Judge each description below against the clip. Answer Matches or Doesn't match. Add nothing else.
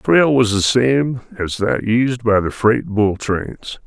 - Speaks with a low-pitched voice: Matches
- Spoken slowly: Doesn't match